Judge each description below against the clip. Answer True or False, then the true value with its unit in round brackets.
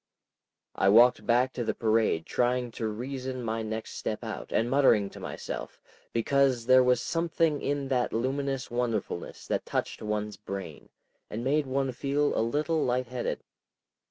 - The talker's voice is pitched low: True (125 Hz)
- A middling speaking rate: True (155 wpm)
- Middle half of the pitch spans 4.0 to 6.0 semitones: False (3.4 semitones)